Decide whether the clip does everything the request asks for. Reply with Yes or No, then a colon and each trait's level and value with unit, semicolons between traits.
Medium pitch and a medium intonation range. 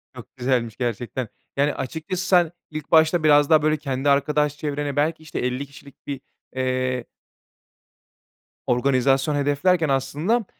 Yes: medium, 145 Hz; average, 3.0 semitones